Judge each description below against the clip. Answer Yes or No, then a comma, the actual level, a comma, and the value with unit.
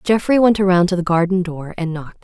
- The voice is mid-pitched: Yes, medium, 180 Hz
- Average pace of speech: No, fast, 240 wpm